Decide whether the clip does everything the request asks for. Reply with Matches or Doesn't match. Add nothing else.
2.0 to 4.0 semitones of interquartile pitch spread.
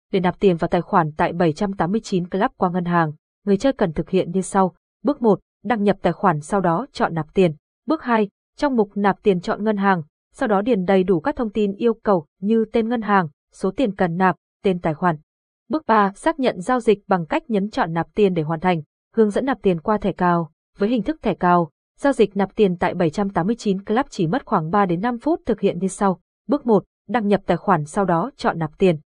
Matches